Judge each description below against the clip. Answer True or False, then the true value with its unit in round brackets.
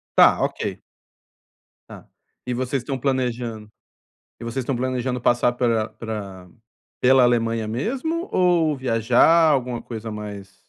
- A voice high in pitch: False (120 Hz)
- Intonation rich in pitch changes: False (2.8 semitones)